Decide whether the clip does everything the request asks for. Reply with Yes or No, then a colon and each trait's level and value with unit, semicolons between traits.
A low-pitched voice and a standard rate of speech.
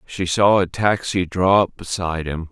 Yes: very low, 90 Hz; average, 190 wpm